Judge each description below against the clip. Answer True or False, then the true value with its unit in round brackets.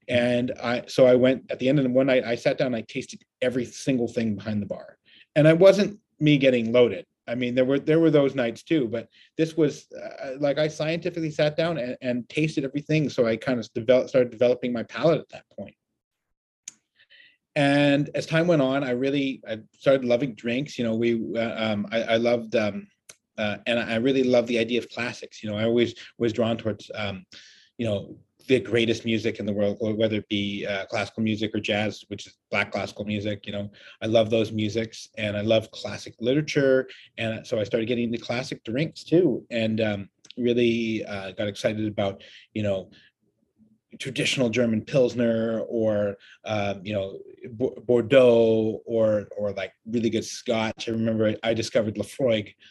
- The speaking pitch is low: True (115 Hz)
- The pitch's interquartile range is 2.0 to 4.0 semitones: True (3.3 semitones)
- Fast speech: False (190 wpm)